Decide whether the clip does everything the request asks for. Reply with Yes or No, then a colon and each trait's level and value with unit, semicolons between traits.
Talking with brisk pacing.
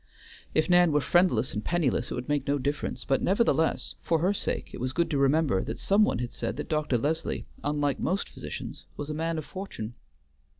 Yes: fast, 210 wpm